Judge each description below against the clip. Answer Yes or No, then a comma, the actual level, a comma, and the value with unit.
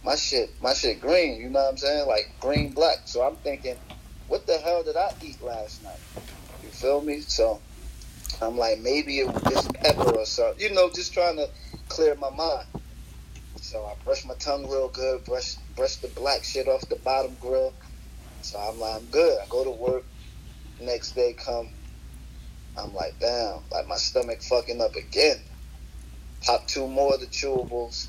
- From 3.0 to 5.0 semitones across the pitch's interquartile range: No, wide, 5.4 semitones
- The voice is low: Yes, low, 130 Hz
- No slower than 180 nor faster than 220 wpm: Yes, average, 190 wpm